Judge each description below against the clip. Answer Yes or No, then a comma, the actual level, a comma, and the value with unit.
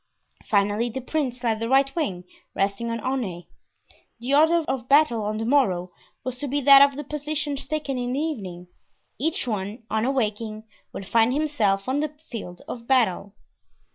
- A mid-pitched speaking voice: No, high, 245 Hz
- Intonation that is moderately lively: Yes, average, 4.9 semitones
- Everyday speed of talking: Yes, average, 170 wpm